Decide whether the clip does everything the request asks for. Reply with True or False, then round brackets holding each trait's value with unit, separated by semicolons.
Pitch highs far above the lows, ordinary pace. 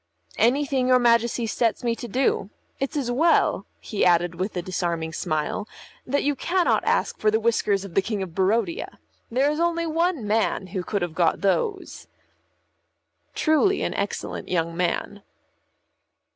True (6.8 semitones; 160 wpm)